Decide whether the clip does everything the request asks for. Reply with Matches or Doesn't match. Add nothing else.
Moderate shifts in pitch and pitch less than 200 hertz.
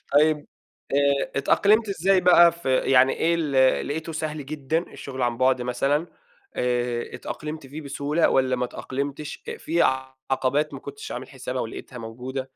Matches